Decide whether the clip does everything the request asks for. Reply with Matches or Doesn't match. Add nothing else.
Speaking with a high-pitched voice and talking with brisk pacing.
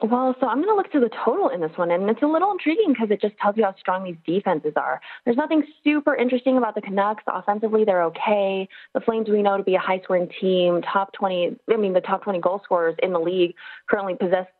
Matches